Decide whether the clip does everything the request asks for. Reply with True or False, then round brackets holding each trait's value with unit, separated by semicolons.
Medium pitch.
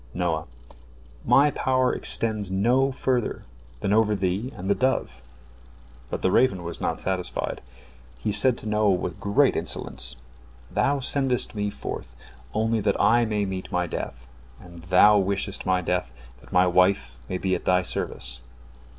False (100 Hz)